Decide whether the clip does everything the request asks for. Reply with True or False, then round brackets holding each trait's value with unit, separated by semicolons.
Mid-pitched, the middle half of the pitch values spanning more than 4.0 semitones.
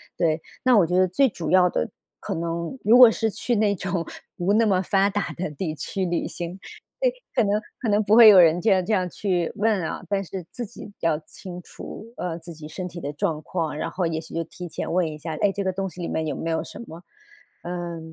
False (180 Hz; 3.5 semitones)